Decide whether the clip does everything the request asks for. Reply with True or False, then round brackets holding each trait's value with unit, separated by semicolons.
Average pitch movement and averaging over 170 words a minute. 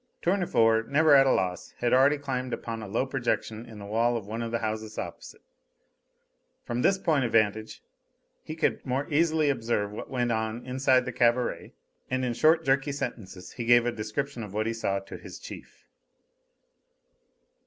True (3.5 semitones; 180 wpm)